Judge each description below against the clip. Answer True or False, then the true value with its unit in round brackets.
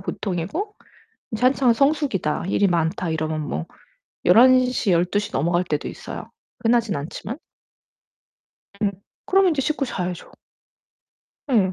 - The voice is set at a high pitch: True (205 Hz)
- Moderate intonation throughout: False (6.9 semitones)